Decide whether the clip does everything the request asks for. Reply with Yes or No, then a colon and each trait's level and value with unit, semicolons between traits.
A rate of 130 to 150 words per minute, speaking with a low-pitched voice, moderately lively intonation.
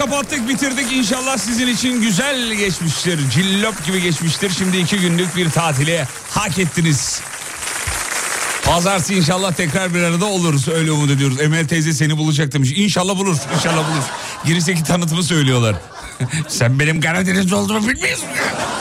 No: average, 135 wpm; medium, 175 Hz; average, 4.1 semitones